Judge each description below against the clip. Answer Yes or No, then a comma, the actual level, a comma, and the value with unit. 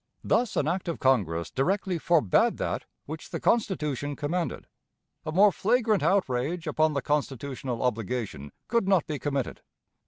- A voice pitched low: No, medium, 150 Hz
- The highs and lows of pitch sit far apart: Yes, wide, 6.1 semitones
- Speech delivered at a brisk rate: No, average, 145 wpm